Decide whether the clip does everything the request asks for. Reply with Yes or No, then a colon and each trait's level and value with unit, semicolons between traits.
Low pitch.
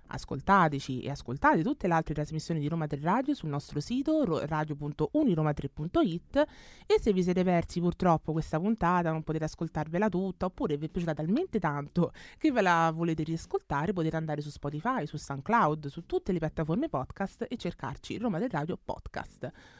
No: medium, 165 Hz